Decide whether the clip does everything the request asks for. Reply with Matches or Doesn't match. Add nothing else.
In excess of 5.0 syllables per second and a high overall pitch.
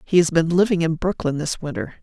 Doesn't match